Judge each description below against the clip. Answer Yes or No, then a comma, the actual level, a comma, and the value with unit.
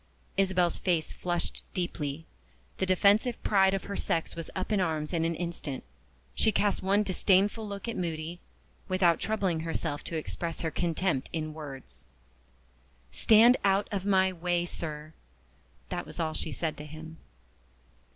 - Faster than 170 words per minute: No, average, 150 wpm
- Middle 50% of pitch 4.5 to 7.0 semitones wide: No, average, 3.3 semitones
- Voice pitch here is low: No, medium, 175 Hz